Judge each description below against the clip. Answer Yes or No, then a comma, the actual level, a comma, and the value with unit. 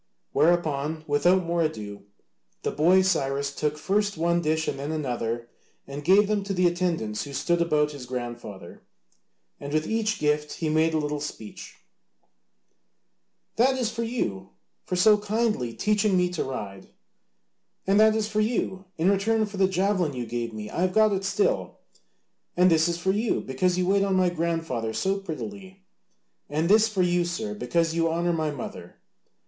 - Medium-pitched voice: Yes, medium, 170 Hz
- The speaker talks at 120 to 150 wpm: No, average, 175 wpm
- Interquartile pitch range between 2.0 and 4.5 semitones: No, average, 5.1 semitones